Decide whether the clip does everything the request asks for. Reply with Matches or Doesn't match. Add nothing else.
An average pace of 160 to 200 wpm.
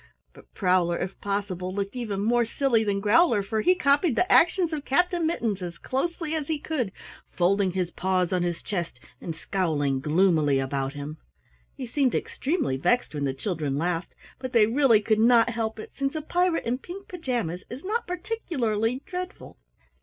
Matches